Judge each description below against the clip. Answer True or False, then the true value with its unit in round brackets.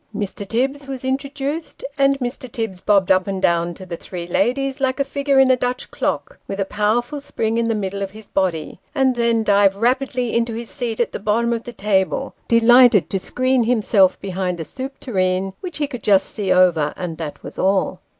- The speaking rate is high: True (210 wpm)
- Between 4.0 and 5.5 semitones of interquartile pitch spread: True (5.2 semitones)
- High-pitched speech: True (225 Hz)